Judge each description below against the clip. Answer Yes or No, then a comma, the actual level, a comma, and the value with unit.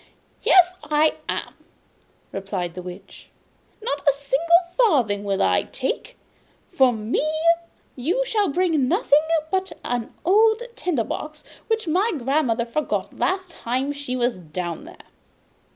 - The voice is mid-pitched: No, very high, 290 Hz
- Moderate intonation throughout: No, wide, 7.6 semitones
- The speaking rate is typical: No, slow, 130 wpm